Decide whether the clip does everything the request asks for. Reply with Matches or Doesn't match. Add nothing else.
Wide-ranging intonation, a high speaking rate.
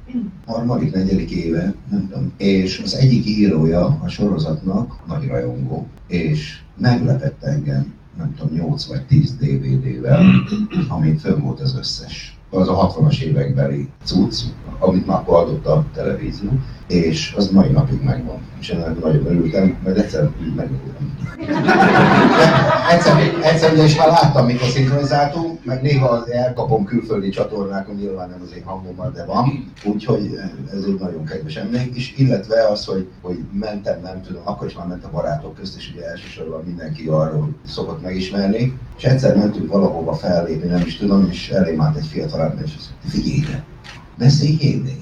Doesn't match